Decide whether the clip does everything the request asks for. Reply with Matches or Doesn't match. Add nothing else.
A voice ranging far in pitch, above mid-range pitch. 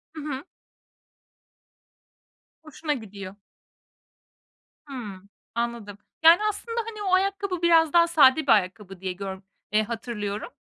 Matches